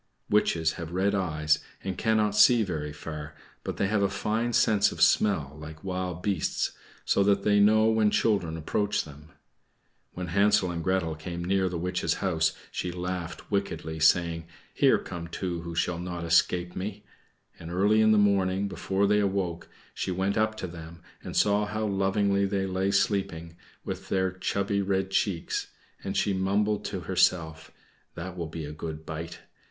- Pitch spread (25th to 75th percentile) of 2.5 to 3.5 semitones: Yes, average, 3.1 semitones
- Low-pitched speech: Yes, very low, 95 Hz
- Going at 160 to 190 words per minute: Yes, average, 170 wpm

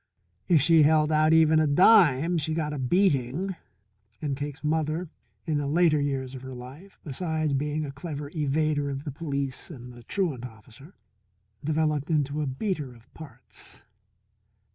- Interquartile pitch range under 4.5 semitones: Yes, narrow, 2.6 semitones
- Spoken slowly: No, average, 160 wpm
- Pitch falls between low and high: Yes, medium, 150 Hz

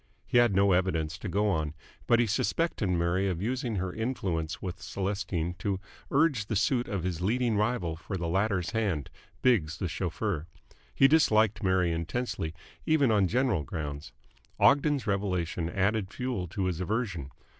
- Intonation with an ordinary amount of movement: Yes, average, 4.7 semitones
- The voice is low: Yes, very low, 95 Hz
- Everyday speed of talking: Yes, average, 160 wpm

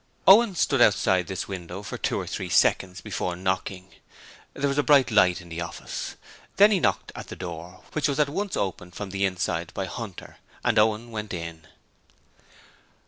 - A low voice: Yes, very low, 95 Hz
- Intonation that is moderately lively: No, wide, 6.7 semitones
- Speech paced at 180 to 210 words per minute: Yes, average, 185 wpm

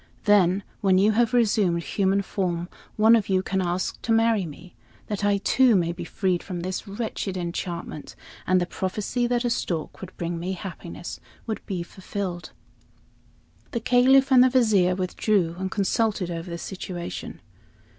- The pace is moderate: Yes, average, 165 wpm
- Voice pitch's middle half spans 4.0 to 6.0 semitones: No, average, 3.6 semitones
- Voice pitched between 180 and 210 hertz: Yes, high, 190 Hz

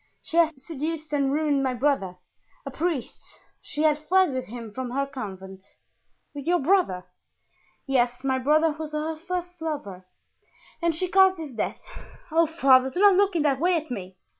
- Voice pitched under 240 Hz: No, very high, 295 Hz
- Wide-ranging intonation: No, average, 4.3 semitones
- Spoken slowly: No, average, 175 wpm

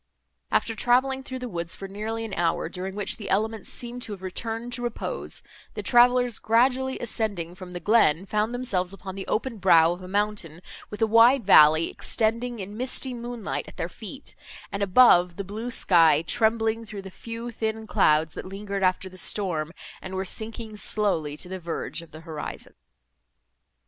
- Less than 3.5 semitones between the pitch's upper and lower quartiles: No, average, 4.1 semitones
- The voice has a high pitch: Yes, high, 210 Hz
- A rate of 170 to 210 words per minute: Yes, average, 180 wpm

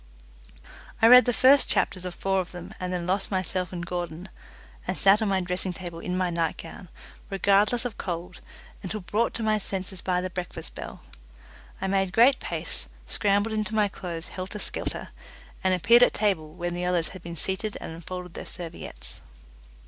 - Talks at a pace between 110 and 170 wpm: No, average, 180 wpm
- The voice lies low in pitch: No, medium, 185 Hz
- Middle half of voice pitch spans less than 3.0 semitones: Yes, narrow, 2.6 semitones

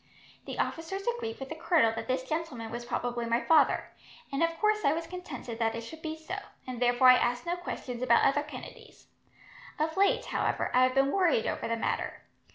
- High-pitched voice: Yes, very high, 280 Hz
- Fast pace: Yes, fast, 210 wpm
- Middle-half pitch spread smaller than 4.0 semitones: No, wide, 5.4 semitones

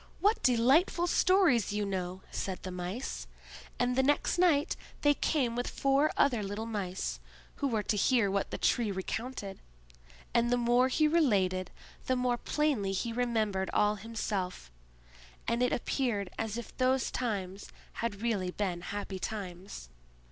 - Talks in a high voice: Yes, high, 230 Hz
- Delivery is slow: No, average, 150 wpm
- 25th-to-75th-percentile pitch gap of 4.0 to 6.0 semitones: Yes, average, 4.6 semitones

